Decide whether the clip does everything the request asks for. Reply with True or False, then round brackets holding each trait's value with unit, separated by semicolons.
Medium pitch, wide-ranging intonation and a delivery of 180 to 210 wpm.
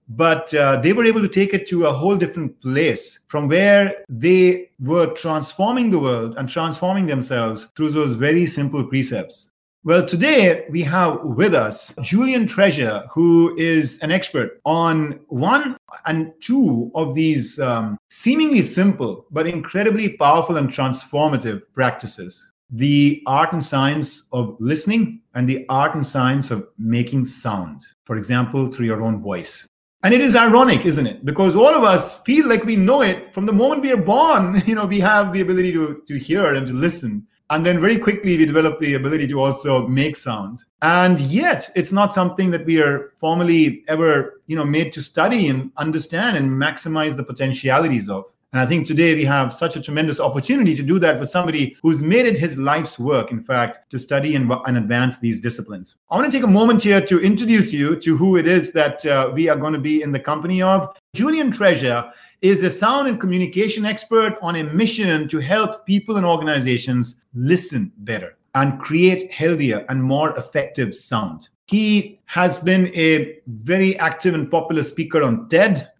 True (160 Hz; 5.7 semitones; 185 wpm)